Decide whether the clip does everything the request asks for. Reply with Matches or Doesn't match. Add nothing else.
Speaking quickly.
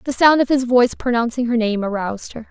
Matches